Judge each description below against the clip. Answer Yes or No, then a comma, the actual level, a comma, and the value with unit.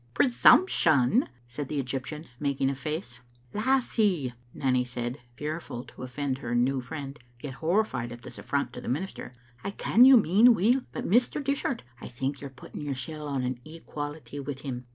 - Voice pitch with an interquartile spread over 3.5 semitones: Yes, wide, 5.4 semitones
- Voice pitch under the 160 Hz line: Yes, medium, 140 Hz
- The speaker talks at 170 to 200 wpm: Yes, average, 180 wpm